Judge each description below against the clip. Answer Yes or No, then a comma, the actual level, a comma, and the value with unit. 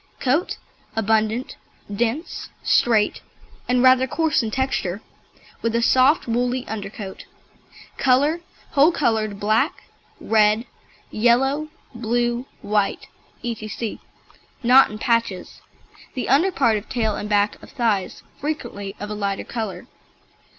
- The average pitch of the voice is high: Yes, high, 235 Hz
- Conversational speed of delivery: No, slow, 115 wpm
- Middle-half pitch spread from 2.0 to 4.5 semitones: Yes, average, 3.4 semitones